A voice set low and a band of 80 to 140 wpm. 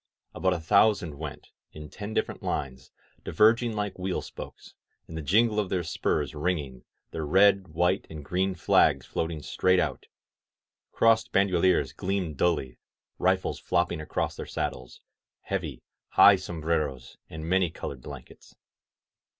Yes: very low, 90 Hz; slow, 135 wpm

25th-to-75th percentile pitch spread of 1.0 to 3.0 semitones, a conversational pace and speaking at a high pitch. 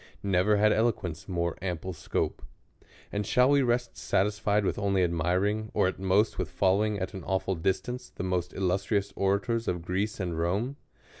No: average, 2.7 semitones; average, 165 wpm; very low, 95 Hz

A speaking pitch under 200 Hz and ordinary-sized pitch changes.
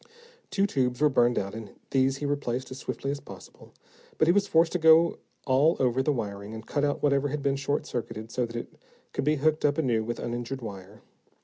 Yes: low, 135 Hz; average, 3.8 semitones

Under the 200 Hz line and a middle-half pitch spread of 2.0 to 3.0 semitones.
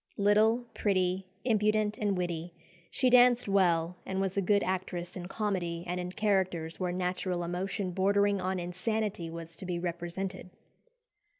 Yes: medium, 185 Hz; narrow, 2.5 semitones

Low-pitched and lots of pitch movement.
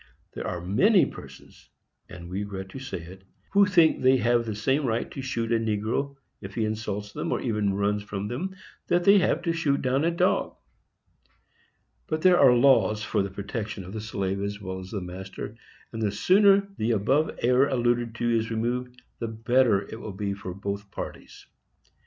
No: low, 115 Hz; average, 4.8 semitones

